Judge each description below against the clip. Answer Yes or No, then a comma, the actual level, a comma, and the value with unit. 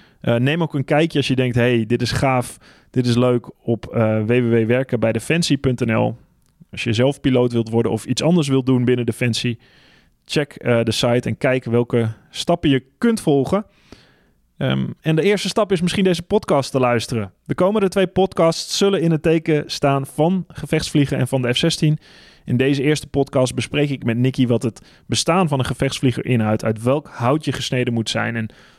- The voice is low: Yes, low, 130 Hz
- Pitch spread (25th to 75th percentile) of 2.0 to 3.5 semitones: No, average, 4.4 semitones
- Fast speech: No, average, 190 wpm